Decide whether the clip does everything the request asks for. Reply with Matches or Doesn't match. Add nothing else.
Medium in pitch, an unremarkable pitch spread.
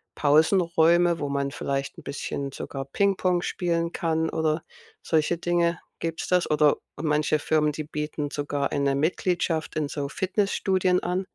Matches